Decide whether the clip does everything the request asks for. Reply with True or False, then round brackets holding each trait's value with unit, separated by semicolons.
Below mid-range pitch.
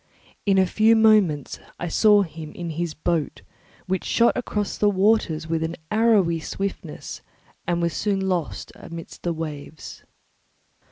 False (175 Hz)